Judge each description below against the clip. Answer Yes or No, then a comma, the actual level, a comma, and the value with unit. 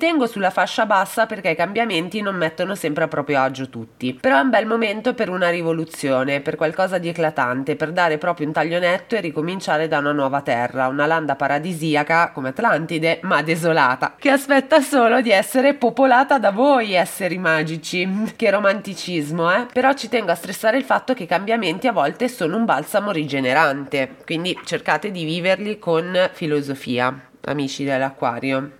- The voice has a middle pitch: Yes, medium, 170 Hz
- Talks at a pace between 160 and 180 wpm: Yes, fast, 170 wpm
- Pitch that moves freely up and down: Yes, wide, 6.0 semitones